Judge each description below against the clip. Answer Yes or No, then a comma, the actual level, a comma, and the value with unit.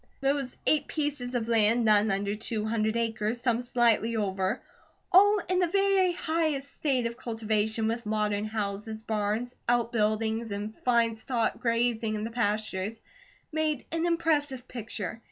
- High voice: Yes, high, 230 Hz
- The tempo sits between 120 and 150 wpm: Yes, average, 145 wpm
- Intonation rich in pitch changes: No, average, 3.5 semitones